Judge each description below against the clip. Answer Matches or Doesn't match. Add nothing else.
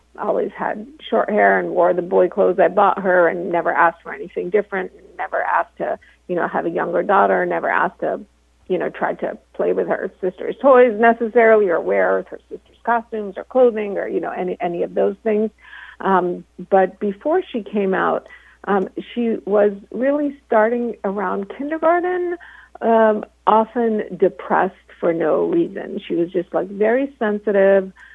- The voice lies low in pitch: Doesn't match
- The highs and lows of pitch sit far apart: Doesn't match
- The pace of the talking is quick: Doesn't match